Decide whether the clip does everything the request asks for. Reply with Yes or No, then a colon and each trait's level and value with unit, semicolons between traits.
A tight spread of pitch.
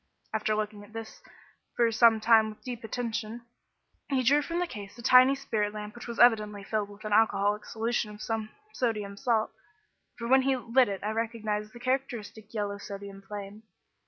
Yes: narrow, 2.3 semitones